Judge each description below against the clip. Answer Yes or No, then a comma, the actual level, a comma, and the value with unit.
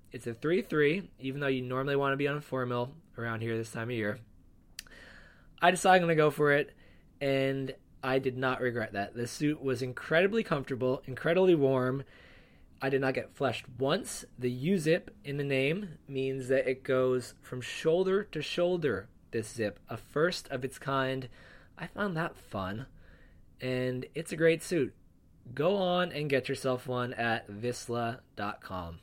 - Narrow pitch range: No, average, 3.8 semitones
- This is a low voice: Yes, low, 130 Hz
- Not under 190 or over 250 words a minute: No, average, 180 wpm